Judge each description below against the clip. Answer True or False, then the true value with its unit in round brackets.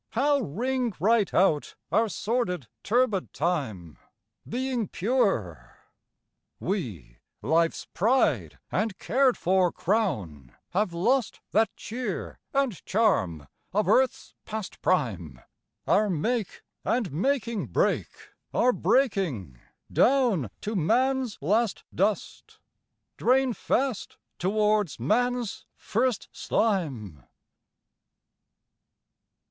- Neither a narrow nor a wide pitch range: False (7.0 semitones)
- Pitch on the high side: True (210 Hz)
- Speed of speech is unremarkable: False (90 wpm)